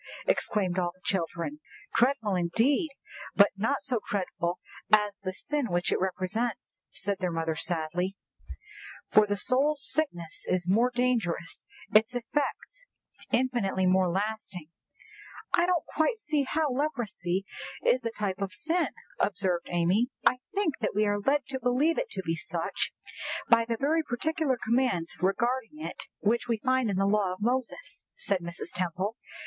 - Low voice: No, high, 215 Hz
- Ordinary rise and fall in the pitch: No, wide, 5.8 semitones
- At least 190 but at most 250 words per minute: No, average, 155 wpm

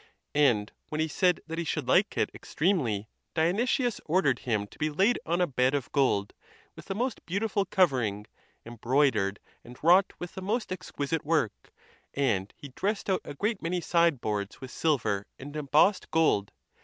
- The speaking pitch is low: No, medium, 155 Hz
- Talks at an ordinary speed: Yes, average, 170 wpm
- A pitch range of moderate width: No, wide, 6.9 semitones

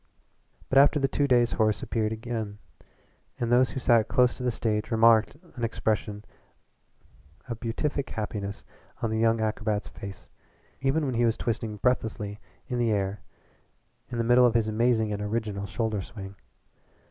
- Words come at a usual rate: Yes, average, 160 wpm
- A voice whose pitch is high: No, low, 115 Hz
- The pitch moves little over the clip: Yes, narrow, 2.3 semitones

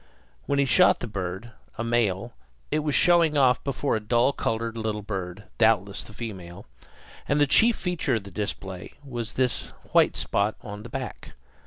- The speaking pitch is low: Yes, low, 115 Hz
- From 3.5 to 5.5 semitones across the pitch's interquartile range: Yes, average, 4.8 semitones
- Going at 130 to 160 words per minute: No, average, 175 wpm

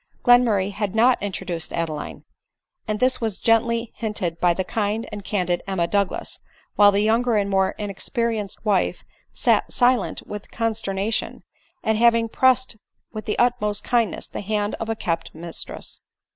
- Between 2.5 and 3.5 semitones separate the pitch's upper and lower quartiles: Yes, average, 2.9 semitones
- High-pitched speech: Yes, high, 210 Hz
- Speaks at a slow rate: No, average, 160 wpm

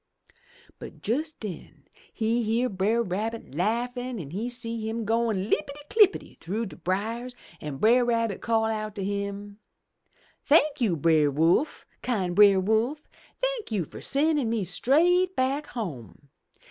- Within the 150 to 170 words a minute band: No, average, 140 wpm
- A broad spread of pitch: No, average, 4.2 semitones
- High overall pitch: Yes, high, 225 Hz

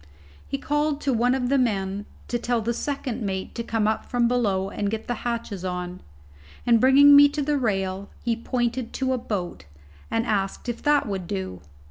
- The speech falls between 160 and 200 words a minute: Yes, average, 195 wpm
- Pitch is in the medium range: No, high, 235 Hz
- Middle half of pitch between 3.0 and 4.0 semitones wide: No, average, 4.7 semitones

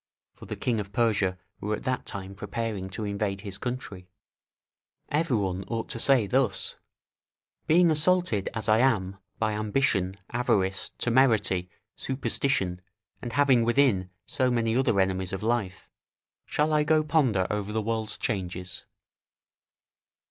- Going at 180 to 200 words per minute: No, average, 140 wpm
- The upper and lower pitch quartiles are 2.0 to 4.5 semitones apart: No, average, 4.9 semitones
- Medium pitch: No, low, 110 Hz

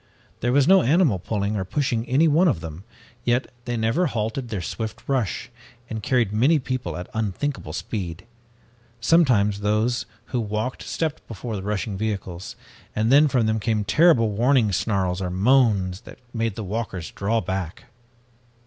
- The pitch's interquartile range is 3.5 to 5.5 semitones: Yes, average, 4.3 semitones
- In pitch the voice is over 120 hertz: No, low, 110 Hz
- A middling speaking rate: Yes, average, 160 wpm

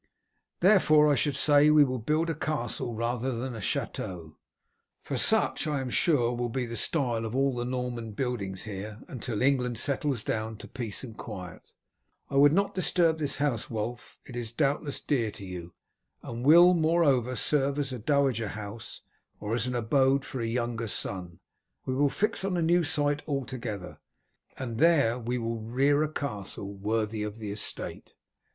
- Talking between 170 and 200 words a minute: Yes, average, 175 wpm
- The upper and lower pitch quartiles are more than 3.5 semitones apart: Yes, average, 4.4 semitones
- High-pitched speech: No, low, 125 Hz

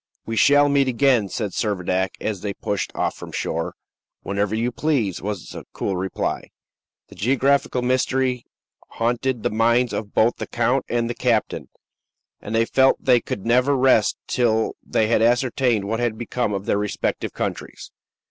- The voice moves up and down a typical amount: Yes, average, 3.3 semitones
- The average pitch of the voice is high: No, low, 115 Hz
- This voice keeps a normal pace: Yes, average, 165 wpm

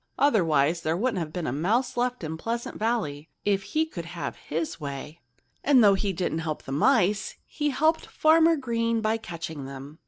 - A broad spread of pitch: Yes, wide, 7.1 semitones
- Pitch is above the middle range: Yes, high, 195 Hz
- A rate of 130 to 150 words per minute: No, average, 185 wpm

